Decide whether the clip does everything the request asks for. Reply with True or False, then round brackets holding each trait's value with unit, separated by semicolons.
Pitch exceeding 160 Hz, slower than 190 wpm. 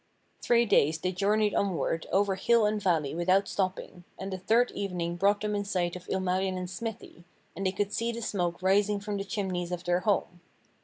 False (190 Hz; 195 wpm)